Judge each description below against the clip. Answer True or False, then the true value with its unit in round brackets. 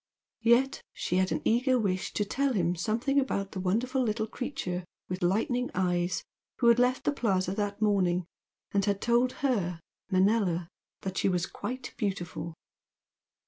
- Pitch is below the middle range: False (205 Hz)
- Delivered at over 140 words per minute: True (155 wpm)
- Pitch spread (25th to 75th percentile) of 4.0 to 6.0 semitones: True (5.0 semitones)